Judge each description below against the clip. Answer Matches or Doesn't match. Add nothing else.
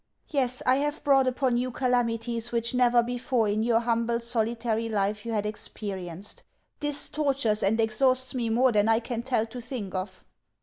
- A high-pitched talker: Matches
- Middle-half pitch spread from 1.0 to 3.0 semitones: Matches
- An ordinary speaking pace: Matches